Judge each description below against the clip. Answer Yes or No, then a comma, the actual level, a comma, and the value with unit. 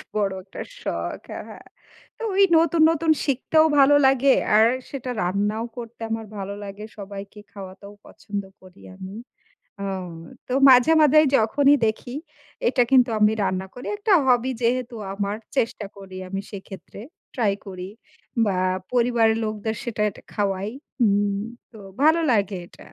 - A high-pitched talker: Yes, high, 220 Hz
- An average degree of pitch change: Yes, average, 4.3 semitones